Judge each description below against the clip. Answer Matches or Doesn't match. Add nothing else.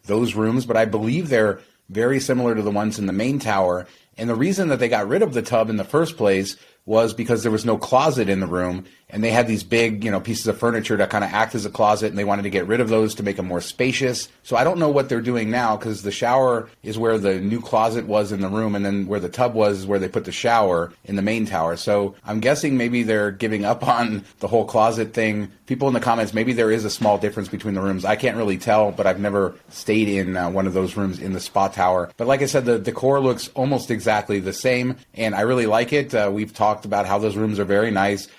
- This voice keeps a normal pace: Doesn't match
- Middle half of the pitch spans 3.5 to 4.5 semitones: Doesn't match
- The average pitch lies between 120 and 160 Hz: Doesn't match